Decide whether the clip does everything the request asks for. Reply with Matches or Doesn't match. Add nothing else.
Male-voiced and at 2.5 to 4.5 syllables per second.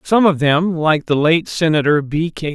Matches